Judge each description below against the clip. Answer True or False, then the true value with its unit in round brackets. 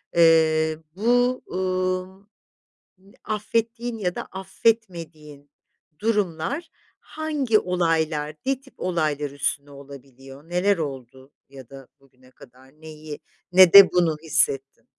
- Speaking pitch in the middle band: True (165 Hz)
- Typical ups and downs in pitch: False (5.8 semitones)